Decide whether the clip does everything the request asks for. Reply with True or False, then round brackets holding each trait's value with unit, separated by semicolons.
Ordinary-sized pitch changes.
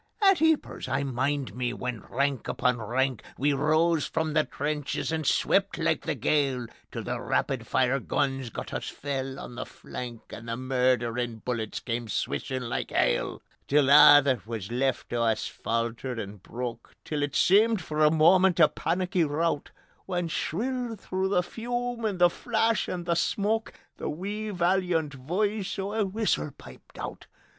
False (6.6 semitones)